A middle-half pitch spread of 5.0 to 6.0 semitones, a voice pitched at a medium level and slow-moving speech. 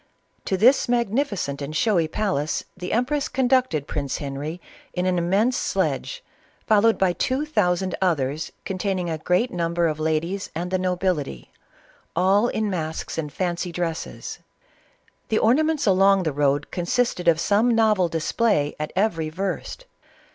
No: average, 5.3 semitones; medium, 180 Hz; average, 145 wpm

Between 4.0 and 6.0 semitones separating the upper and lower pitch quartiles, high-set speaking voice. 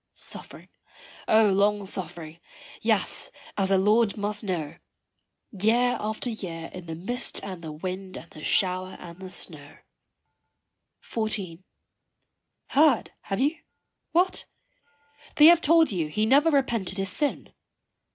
Yes: average, 4.5 semitones; high, 195 Hz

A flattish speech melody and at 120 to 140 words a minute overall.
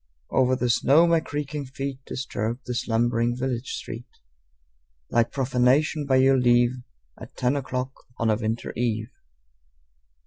Yes: narrow, 2.2 semitones; slow, 135 wpm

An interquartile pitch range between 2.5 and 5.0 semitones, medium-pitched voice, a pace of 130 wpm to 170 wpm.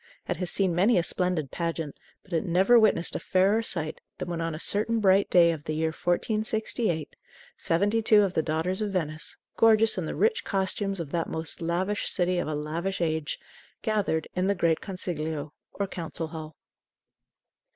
No: average, 3.7 semitones; medium, 175 Hz; average, 180 wpm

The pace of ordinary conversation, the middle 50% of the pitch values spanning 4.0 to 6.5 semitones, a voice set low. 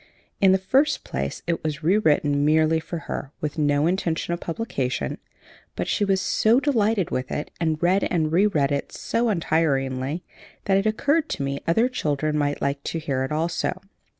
No: average, 180 wpm; average, 5.1 semitones; medium, 160 Hz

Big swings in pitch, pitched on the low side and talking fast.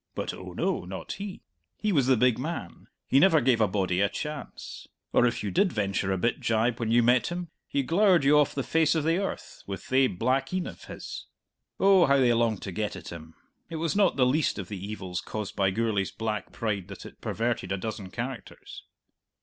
Yes: wide, 6.7 semitones; low, 120 Hz; fast, 220 wpm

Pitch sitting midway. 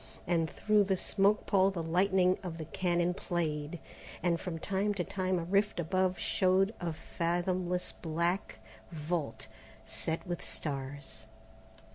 Yes: medium, 175 Hz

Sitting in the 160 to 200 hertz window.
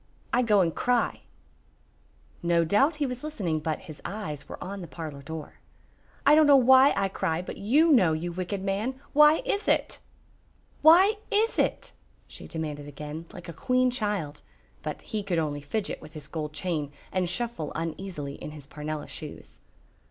Yes: medium, 185 Hz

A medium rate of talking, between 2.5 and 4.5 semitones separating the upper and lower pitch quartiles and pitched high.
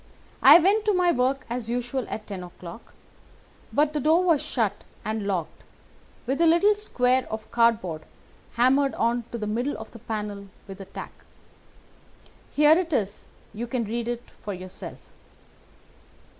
No: average, 155 wpm; average, 5.3 semitones; high, 240 Hz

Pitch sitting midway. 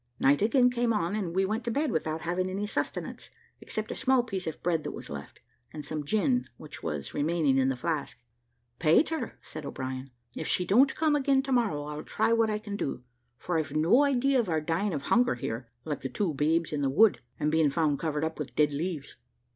Yes: medium, 170 Hz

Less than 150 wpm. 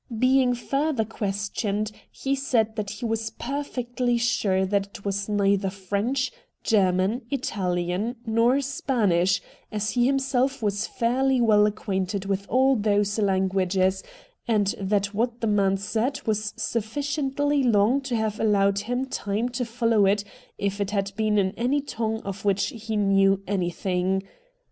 Yes: average, 140 wpm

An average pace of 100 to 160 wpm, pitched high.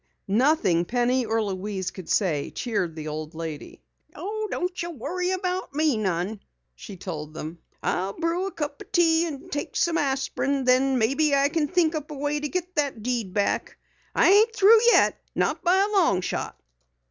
No: average, 180 wpm; very high, 275 Hz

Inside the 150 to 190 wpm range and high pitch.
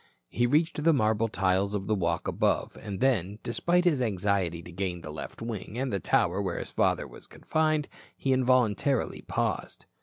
No: average, 180 wpm; low, 110 Hz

